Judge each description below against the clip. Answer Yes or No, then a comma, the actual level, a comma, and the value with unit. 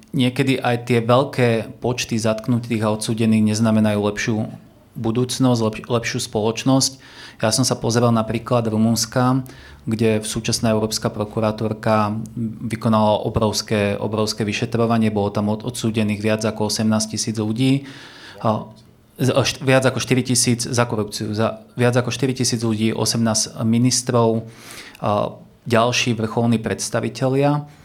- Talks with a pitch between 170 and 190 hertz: No, low, 115 Hz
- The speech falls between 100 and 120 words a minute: No, average, 140 wpm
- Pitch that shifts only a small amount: Yes, narrow, 2.0 semitones